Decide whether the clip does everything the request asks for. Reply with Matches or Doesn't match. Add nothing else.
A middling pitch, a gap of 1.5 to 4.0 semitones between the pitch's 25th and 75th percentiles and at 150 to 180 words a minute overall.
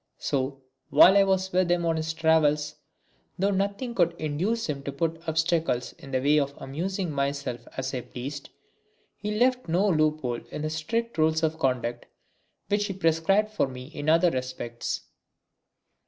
Doesn't match